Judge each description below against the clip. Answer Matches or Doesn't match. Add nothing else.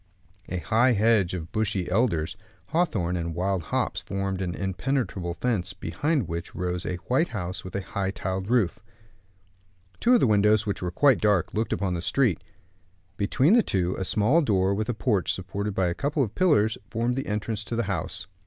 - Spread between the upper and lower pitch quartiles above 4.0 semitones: Matches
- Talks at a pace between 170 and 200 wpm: Matches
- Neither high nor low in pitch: Doesn't match